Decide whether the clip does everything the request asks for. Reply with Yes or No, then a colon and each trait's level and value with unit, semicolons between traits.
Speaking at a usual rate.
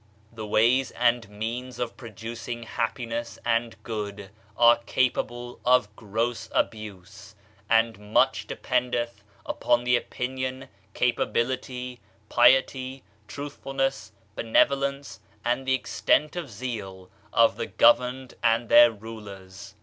No: slow, 105 wpm